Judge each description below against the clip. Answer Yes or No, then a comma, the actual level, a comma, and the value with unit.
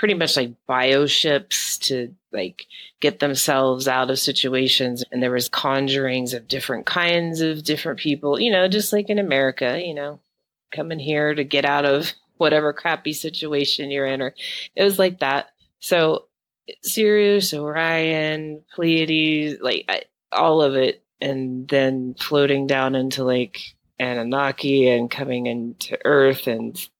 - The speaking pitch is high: No, medium, 140 Hz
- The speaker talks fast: No, average, 150 wpm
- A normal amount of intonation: Yes, average, 3.0 semitones